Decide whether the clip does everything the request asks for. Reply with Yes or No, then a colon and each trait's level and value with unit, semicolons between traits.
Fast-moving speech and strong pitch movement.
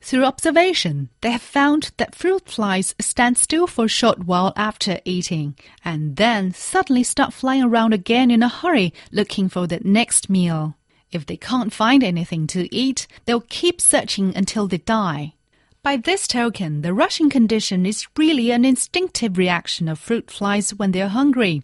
No: average, 170 wpm; wide, 6.1 semitones